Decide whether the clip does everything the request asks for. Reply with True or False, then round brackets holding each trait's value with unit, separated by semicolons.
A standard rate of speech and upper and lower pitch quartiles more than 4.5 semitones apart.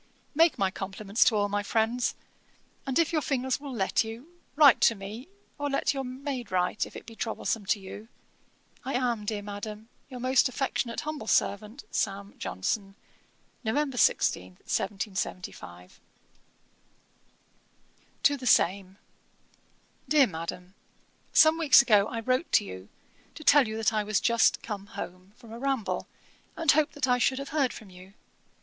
True (155 wpm; 5.0 semitones)